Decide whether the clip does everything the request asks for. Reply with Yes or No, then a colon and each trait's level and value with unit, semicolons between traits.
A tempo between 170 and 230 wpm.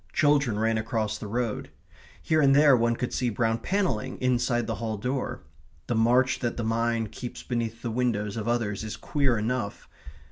Yes: average, 180 wpm